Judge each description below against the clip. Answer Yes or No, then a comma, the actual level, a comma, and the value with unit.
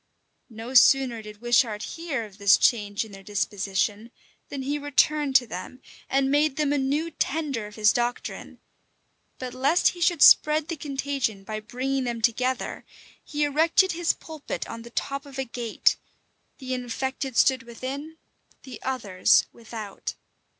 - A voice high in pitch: Yes, very high, 255 Hz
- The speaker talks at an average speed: Yes, average, 155 wpm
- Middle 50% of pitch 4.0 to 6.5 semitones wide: Yes, average, 4.3 semitones